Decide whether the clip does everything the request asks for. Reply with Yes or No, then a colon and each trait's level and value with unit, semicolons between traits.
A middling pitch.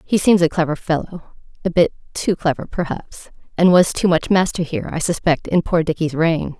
Yes: medium, 165 Hz